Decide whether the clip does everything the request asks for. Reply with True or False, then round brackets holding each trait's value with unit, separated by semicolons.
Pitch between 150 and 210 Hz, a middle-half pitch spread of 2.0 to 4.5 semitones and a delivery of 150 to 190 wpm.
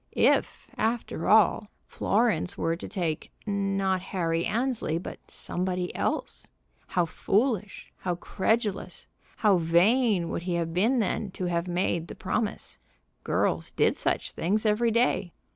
False (190 Hz; 3.9 semitones; 135 wpm)